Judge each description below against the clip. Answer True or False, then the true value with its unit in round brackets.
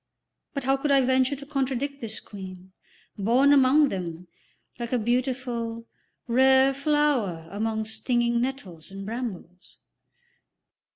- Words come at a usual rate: False (120 wpm)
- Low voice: False (245 Hz)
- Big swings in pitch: False (4.2 semitones)